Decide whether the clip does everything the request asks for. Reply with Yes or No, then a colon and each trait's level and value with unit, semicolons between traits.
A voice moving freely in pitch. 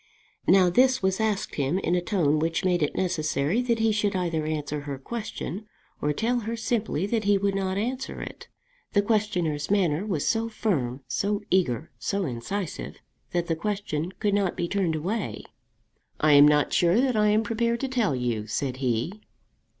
Yes: wide, 5.9 semitones